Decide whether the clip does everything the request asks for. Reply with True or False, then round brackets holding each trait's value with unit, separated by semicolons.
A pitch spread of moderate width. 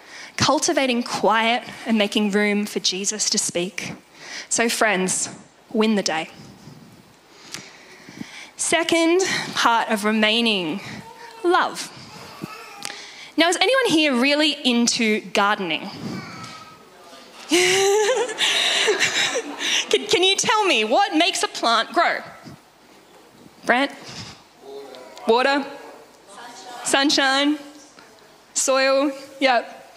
False (7.8 semitones)